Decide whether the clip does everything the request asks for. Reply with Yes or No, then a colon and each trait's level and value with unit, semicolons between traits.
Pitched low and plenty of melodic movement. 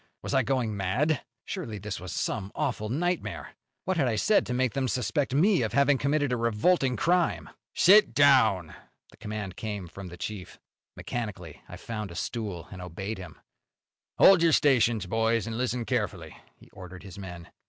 Yes: low, 115 Hz; wide, 5.9 semitones